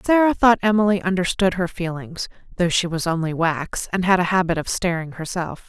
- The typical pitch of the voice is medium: Yes, medium, 180 Hz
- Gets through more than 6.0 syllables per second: No, 5.4 syllables/s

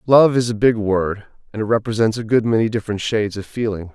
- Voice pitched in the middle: No, low, 110 Hz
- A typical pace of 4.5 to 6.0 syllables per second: No, 6.2 syllables/s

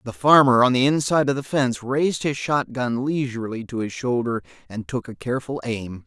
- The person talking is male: Yes, male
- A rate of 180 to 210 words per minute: Yes, average, 200 wpm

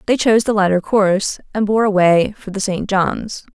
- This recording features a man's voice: No, female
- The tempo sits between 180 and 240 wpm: Yes, fast, 205 wpm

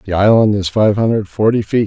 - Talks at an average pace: No, fast, 225 wpm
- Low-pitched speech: Yes, low, 105 Hz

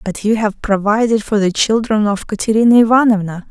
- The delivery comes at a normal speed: Yes, average, 170 wpm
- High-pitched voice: Yes, high, 215 Hz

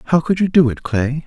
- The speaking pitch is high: No, medium, 150 Hz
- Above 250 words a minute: Yes, fast, 285 wpm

